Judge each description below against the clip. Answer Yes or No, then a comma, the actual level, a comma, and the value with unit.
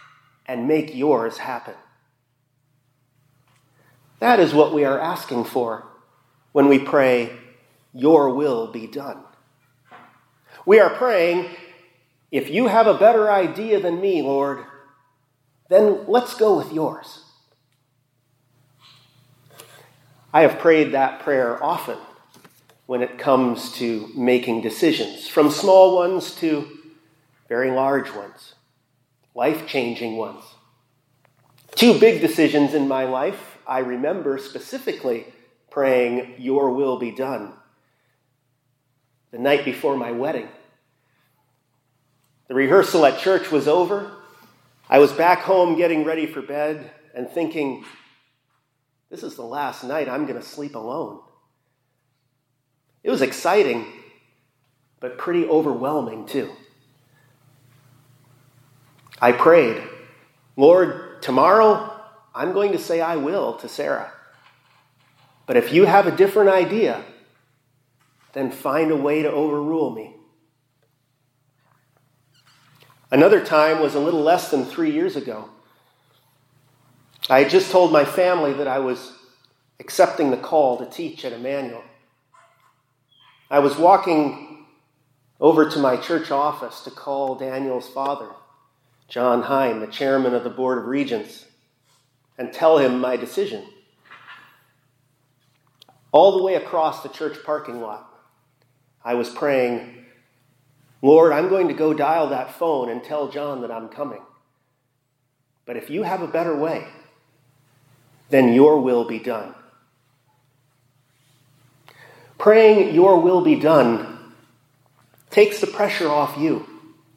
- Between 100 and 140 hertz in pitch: Yes, low, 135 Hz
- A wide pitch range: No, average, 3.2 semitones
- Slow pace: Yes, slow, 120 wpm